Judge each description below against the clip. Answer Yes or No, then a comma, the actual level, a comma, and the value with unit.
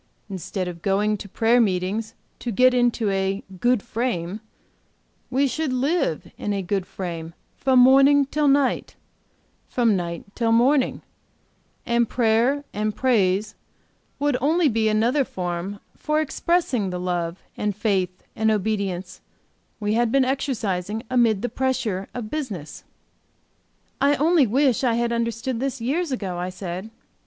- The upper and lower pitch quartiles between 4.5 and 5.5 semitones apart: Yes, average, 5.2 semitones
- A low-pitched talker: No, high, 225 Hz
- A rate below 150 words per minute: Yes, average, 140 wpm